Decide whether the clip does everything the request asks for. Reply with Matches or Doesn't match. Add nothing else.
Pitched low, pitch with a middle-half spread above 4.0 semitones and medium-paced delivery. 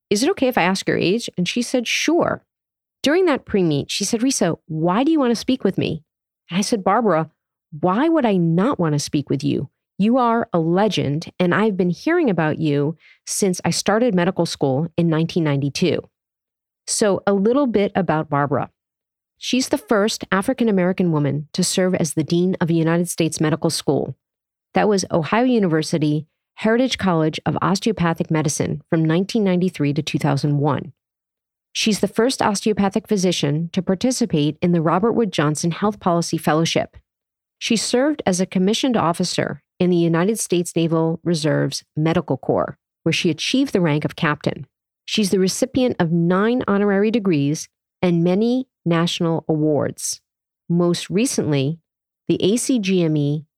Doesn't match